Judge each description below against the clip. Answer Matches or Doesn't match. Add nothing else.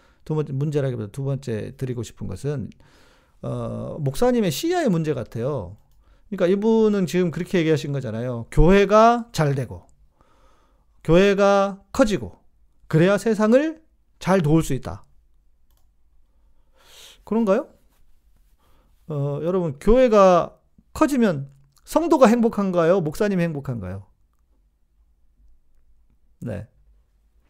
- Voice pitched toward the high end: Doesn't match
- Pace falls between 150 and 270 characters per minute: Matches